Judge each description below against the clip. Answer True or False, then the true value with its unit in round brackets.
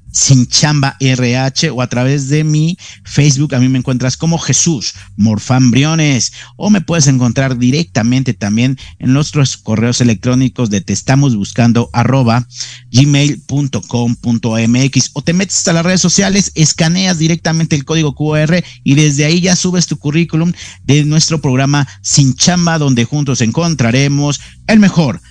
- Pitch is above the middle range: False (135 Hz)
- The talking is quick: False (145 wpm)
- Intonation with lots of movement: False (4.5 semitones)